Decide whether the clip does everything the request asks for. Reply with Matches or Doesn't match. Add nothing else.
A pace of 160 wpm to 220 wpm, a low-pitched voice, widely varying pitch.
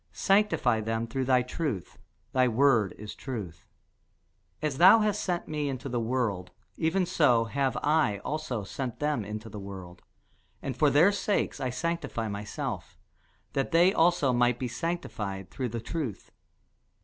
Doesn't match